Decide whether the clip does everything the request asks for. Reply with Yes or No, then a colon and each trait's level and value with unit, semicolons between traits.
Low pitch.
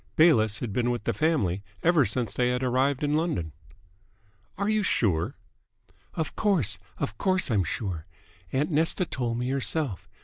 Yes: low, 125 Hz